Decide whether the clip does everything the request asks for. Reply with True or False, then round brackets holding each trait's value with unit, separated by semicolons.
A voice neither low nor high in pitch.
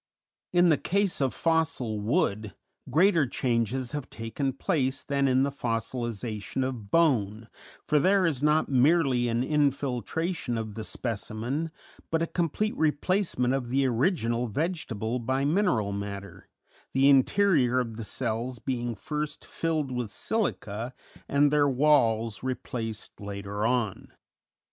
False (130 Hz)